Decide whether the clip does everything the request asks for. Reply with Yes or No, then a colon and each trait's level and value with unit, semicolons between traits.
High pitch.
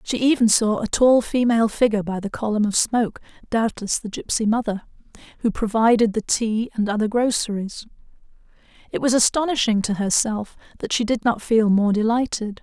Yes: high, 225 Hz